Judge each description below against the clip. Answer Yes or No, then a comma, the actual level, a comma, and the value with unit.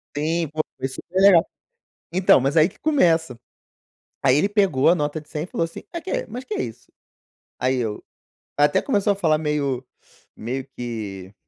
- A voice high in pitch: No, medium, 155 Hz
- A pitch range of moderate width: No, wide, 5.8 semitones